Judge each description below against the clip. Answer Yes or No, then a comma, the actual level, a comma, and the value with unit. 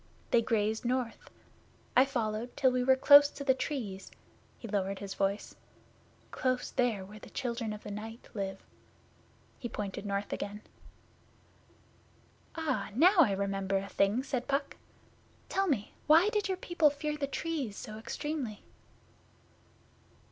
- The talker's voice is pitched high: Yes, high, 240 Hz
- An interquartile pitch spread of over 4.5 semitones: Yes, wide, 5.4 semitones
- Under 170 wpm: Yes, average, 140 wpm